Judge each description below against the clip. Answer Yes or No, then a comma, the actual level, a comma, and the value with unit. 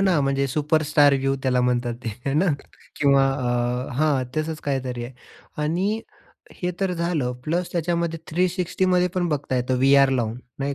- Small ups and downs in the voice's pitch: No, average, 4.6 semitones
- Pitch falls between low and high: Yes, medium, 145 Hz